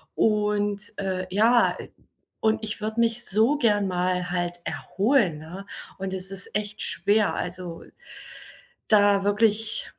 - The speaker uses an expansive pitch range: No, average, 2.9 semitones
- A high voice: Yes, high, 205 Hz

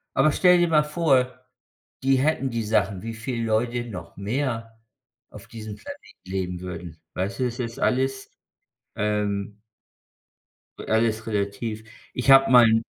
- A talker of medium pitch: No, low, 115 Hz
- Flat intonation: No, average, 4.0 semitones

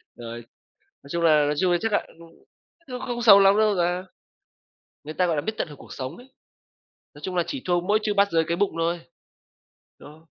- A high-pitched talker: No, medium, 175 Hz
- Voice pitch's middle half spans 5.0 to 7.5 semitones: No, average, 4.4 semitones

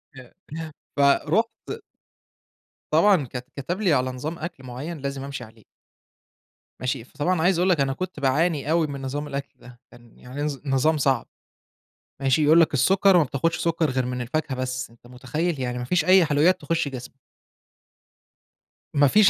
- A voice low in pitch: No, medium, 145 Hz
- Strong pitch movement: No, average, 4.2 semitones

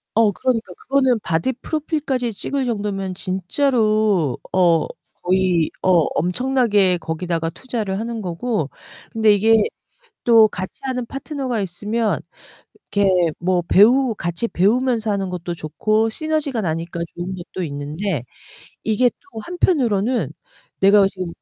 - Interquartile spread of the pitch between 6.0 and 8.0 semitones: No, average, 5.3 semitones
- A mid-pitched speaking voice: No, high, 210 Hz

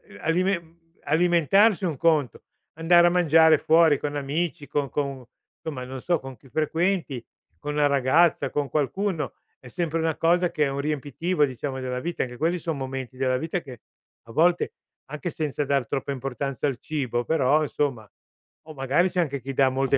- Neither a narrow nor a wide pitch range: Yes, average, 3.7 semitones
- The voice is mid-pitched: Yes, medium, 150 Hz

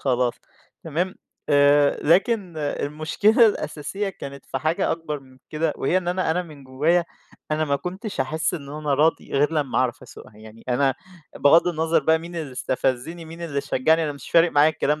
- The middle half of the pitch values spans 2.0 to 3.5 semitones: Yes, average, 3.1 semitones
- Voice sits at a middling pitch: Yes, medium, 155 Hz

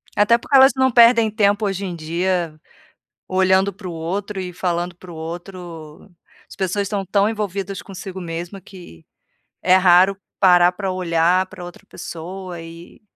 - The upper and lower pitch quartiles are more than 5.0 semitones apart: No, narrow, 2.4 semitones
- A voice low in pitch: No, medium, 185 Hz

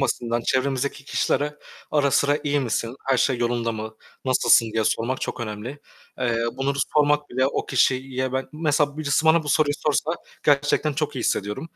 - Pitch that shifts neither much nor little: Yes, average, 3.4 semitones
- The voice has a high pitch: No, low, 135 Hz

